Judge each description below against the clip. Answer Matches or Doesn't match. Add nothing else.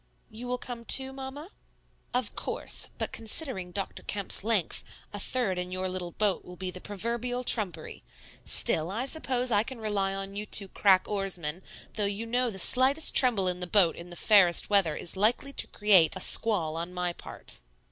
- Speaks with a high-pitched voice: Matches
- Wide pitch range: Doesn't match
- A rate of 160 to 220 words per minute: Matches